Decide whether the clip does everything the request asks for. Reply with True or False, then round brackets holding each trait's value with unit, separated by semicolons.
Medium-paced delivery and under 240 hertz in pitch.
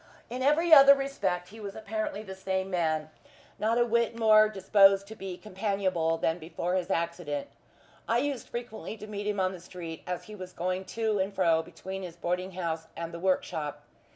True (190 wpm; 190 Hz)